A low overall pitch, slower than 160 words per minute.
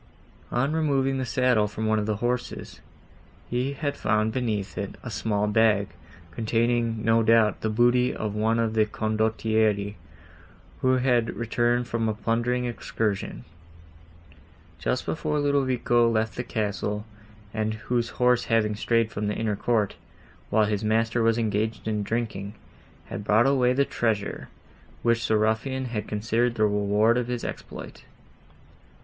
Yes: low, 115 Hz; average, 145 wpm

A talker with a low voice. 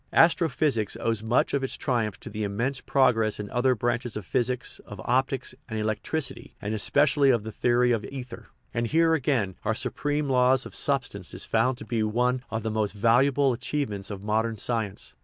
Yes: low, 120 Hz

